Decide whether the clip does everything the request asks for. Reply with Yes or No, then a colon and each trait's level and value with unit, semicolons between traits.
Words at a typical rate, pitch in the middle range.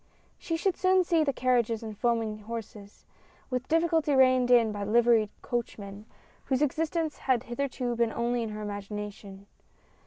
No: average, 150 wpm; high, 240 Hz